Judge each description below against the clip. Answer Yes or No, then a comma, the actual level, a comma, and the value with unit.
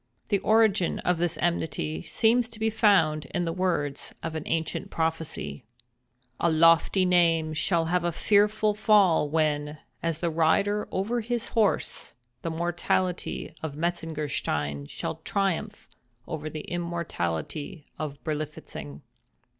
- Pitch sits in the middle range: Yes, medium, 165 Hz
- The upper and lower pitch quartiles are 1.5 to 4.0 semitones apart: Yes, average, 3.7 semitones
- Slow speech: Yes, slow, 125 wpm